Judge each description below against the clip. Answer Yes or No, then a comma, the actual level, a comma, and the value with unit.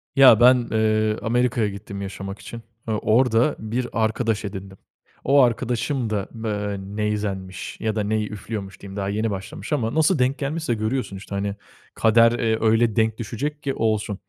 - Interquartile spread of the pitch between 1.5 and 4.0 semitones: Yes, average, 2.9 semitones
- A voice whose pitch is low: Yes, low, 110 Hz